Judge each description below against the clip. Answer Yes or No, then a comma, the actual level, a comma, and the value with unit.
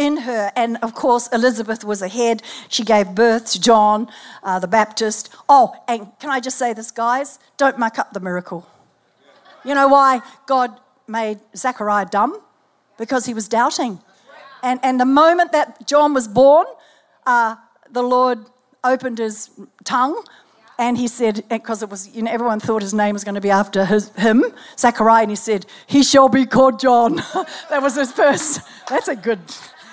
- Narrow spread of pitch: No, average, 3.4 semitones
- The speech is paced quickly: No, average, 180 wpm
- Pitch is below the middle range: No, high, 235 Hz